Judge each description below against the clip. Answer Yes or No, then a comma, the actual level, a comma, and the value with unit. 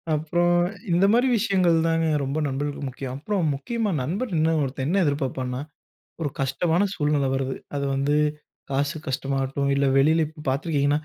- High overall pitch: No, medium, 145 Hz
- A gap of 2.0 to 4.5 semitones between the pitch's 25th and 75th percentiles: Yes, average, 3.7 semitones